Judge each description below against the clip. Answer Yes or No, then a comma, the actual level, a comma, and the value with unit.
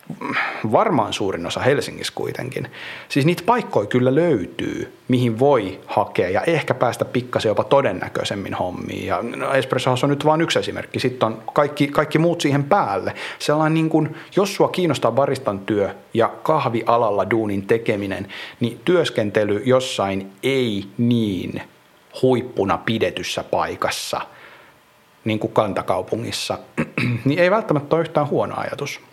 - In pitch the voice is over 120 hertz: Yes, low, 130 Hz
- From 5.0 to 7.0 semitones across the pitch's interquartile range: Yes, wide, 5.6 semitones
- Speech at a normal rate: Yes, average, 130 wpm